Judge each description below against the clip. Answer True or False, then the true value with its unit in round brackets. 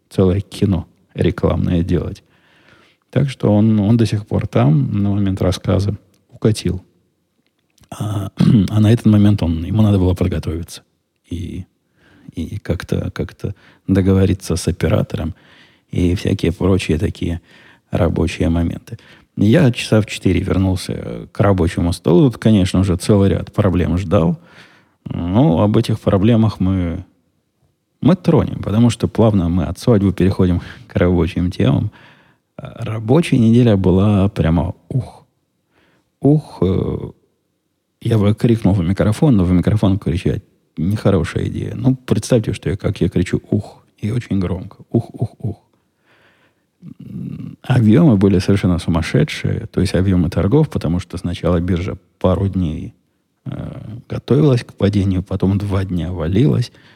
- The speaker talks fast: False (130 wpm)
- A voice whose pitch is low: True (100 Hz)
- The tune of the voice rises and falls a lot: False (3.7 semitones)